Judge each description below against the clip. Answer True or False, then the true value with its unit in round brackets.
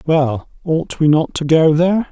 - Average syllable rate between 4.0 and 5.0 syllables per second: True (4.4 syllables/s)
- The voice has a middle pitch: True (160 Hz)